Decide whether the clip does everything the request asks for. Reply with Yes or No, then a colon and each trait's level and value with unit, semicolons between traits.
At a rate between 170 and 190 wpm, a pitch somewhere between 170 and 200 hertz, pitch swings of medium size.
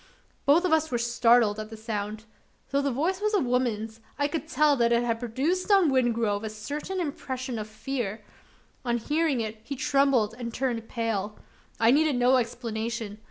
No: average, 180 wpm; high, 240 Hz; average, 4.2 semitones